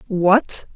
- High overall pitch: Yes, high, 200 Hz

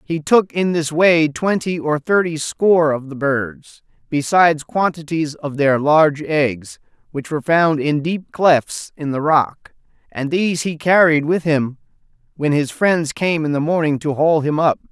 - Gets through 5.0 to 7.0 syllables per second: No, 4.3 syllables/s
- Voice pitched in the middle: Yes, medium, 155 Hz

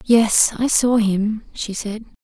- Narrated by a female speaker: Yes, female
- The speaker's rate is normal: Yes, average, 160 wpm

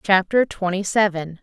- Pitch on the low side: No, high, 190 Hz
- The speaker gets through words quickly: No, slow, 125 wpm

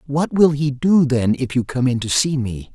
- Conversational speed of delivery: No, fast, 260 wpm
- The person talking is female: No, male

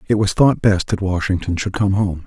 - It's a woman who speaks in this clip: No, male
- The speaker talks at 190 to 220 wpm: No, fast, 240 wpm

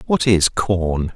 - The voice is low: Yes, low, 100 Hz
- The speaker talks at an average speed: Yes, average, 155 wpm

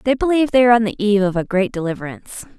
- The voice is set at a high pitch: Yes, high, 215 Hz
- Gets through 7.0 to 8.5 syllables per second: Yes, 8.0 syllables/s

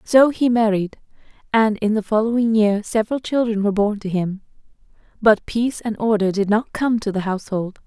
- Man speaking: No, female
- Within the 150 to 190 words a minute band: Yes, average, 185 wpm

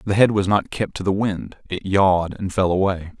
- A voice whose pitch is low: Yes, very low, 95 Hz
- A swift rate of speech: Yes, fast, 245 wpm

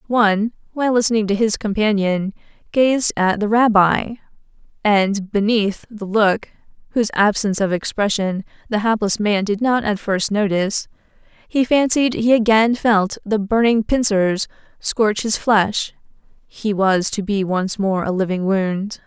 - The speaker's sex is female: Yes, female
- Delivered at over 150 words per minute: No, average, 140 wpm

